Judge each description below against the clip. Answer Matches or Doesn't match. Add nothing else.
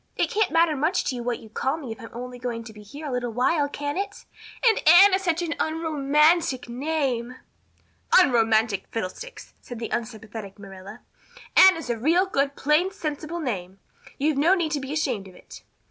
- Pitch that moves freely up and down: Matches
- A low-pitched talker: Doesn't match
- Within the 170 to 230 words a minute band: Matches